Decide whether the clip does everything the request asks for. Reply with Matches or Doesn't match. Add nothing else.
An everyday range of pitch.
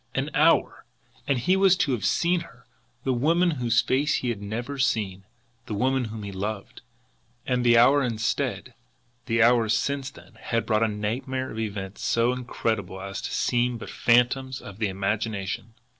Matches